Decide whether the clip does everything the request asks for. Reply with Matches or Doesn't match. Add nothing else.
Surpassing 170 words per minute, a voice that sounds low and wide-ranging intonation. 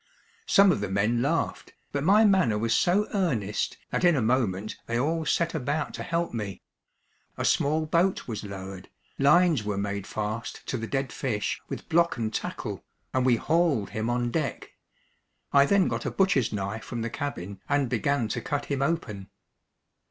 Matches